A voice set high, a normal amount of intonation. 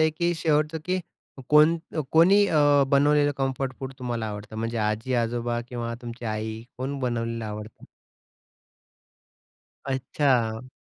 No: low, 125 Hz; average, 4.5 semitones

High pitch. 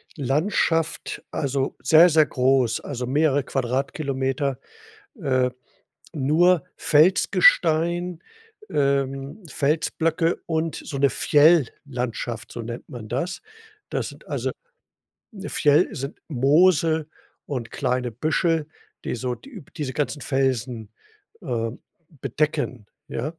No: medium, 140 Hz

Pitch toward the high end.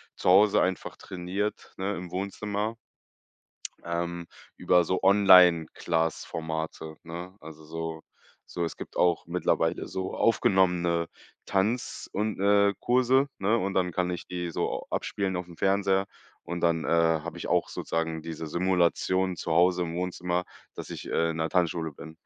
No: very low, 90 Hz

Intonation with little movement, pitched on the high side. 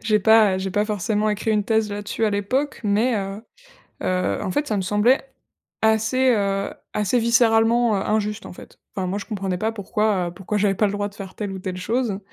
Yes: narrow, 2.2 semitones; high, 210 Hz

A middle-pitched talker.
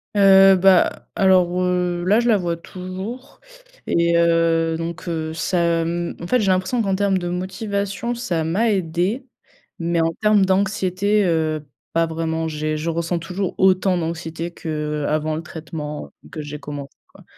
Yes: medium, 175 Hz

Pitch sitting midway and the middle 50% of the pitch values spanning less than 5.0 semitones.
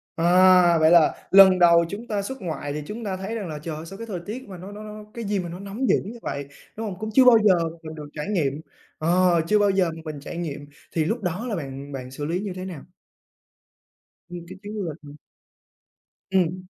Yes: medium, 180 Hz; average, 4.3 semitones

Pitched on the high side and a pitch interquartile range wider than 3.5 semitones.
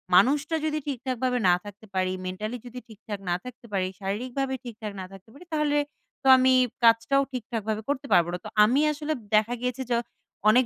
Yes: high, 240 Hz; average, 4.1 semitones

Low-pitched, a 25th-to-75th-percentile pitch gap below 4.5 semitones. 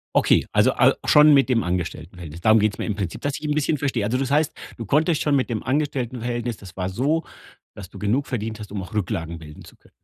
No: low, 115 Hz; wide, 6.3 semitones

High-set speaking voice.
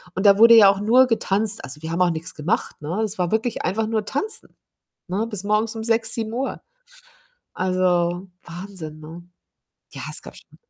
Yes: high, 200 Hz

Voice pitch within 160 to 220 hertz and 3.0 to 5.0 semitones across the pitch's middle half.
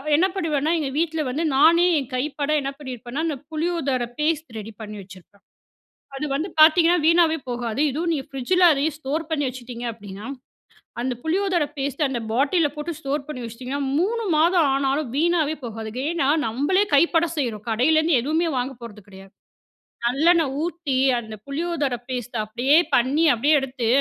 No: very high, 285 Hz; average, 4.7 semitones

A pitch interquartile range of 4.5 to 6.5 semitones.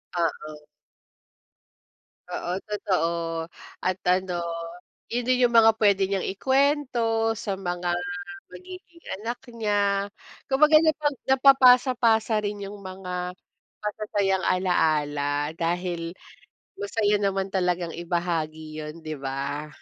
Yes: average, 5.0 semitones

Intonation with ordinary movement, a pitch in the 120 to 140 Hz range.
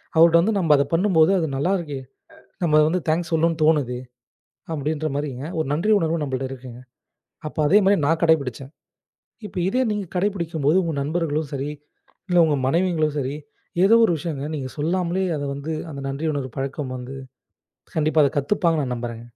No: average, 3.4 semitones; medium, 155 Hz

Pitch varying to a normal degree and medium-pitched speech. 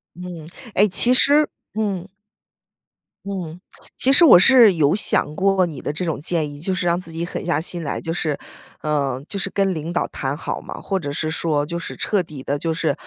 Yes: average, 4.0 semitones; medium, 170 Hz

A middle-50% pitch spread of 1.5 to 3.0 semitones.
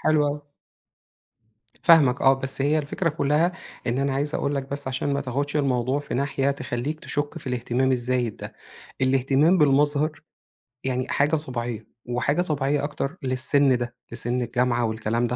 Yes: average, 2.7 semitones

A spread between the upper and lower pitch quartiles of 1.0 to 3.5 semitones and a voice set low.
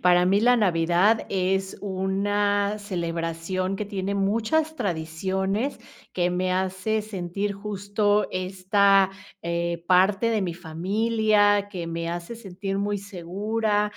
No: narrow, 2.4 semitones; high, 195 Hz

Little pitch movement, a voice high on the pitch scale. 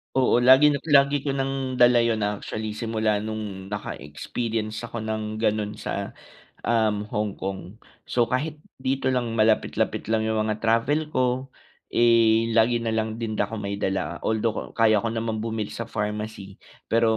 No: narrow, 2.1 semitones; low, 110 Hz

